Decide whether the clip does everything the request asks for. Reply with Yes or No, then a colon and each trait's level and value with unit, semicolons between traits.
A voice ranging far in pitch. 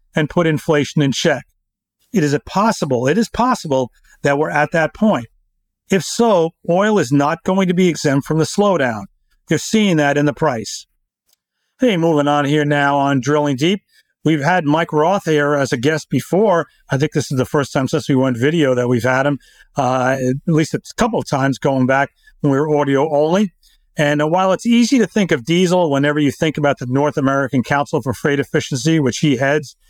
No: average, 3.5 semitones